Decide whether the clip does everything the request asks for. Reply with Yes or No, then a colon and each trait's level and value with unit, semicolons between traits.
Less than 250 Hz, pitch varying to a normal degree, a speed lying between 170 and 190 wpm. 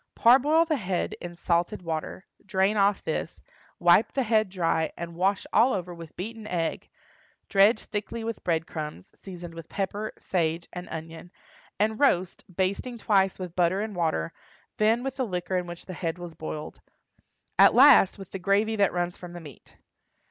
Yes: medium, 185 Hz; average, 3.9 semitones; average, 175 wpm